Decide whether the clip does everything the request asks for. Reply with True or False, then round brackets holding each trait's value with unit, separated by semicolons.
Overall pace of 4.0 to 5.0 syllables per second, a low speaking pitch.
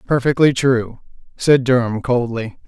True (4.3 syllables/s; 125 Hz)